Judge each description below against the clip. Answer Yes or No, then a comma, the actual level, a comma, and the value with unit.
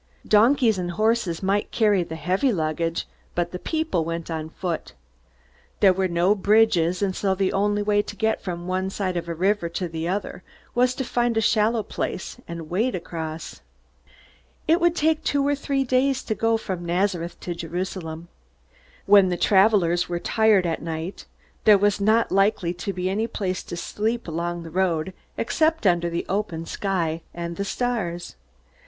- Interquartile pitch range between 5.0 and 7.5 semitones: No, average, 4.2 semitones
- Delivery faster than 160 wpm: Yes, average, 175 wpm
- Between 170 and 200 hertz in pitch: Yes, high, 190 Hz